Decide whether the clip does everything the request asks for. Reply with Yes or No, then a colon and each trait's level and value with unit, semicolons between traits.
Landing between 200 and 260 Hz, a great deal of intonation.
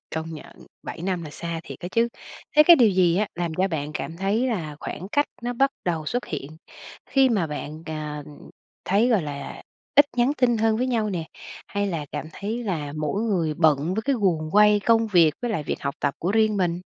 No: medium, 185 Hz; wide, 6.1 semitones